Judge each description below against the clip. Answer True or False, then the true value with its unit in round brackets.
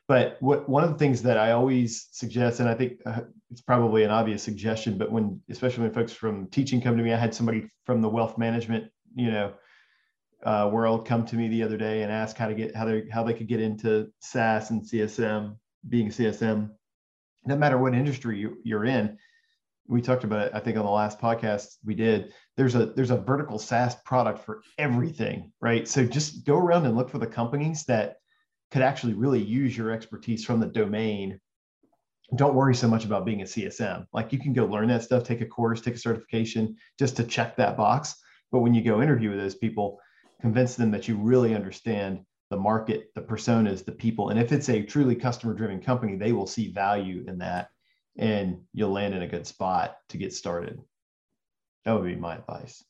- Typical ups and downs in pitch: False (2.3 semitones)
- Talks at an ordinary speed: False (210 wpm)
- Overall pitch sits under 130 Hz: True (115 Hz)